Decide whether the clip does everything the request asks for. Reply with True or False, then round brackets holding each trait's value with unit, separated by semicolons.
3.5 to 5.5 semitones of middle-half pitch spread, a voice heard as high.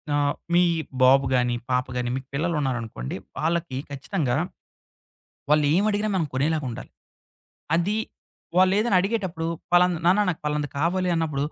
False (5.0 semitones; 155 Hz)